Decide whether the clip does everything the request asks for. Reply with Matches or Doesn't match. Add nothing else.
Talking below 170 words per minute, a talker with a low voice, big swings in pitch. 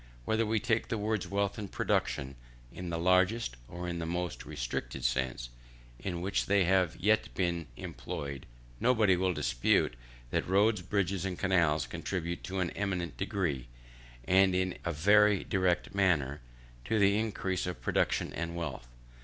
Doesn't match